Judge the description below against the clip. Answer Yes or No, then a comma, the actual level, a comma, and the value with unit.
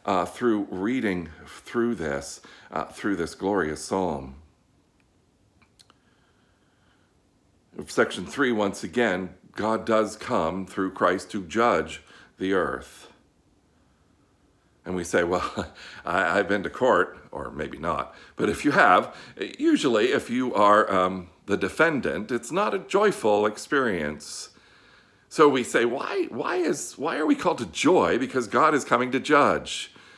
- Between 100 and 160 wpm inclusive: Yes, slow, 135 wpm